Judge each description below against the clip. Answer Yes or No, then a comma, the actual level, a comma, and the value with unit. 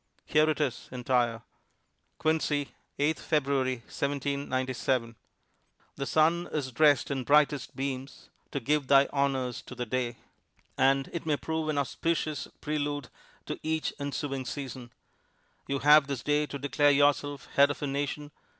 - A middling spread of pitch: No, narrow, 2.1 semitones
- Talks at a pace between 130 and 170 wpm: Yes, average, 140 wpm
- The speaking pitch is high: No, medium, 140 Hz